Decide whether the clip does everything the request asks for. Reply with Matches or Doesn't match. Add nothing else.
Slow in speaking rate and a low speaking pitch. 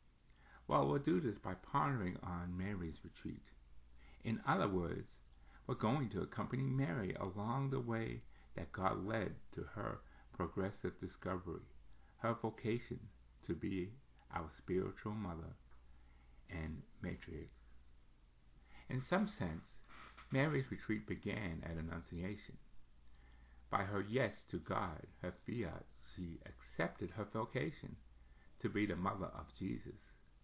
Matches